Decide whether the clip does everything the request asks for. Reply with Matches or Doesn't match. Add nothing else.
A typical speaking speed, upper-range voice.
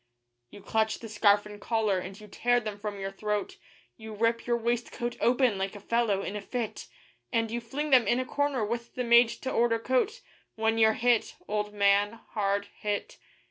Matches